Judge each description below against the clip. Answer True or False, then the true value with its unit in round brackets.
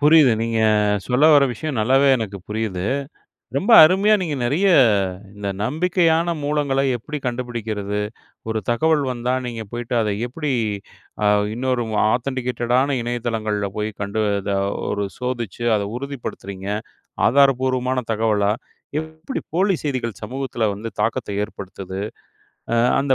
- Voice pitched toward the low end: True (125 Hz)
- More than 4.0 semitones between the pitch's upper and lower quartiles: True (4.4 semitones)